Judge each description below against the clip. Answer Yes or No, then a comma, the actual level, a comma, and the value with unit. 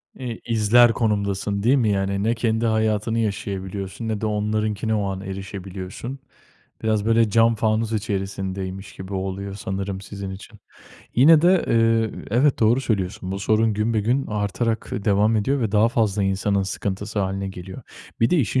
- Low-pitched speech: Yes, low, 105 Hz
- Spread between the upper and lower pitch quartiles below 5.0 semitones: Yes, average, 2.7 semitones